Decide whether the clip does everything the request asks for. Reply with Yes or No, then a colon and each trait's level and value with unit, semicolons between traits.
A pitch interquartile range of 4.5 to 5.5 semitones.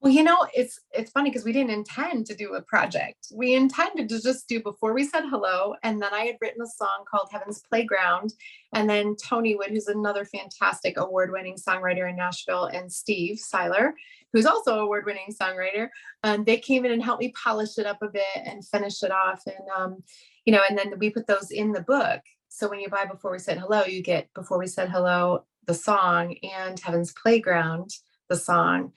No: average, 3.6 semitones